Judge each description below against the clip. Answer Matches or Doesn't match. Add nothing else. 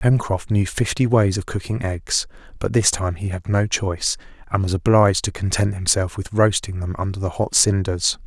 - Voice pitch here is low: Matches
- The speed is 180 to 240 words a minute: Matches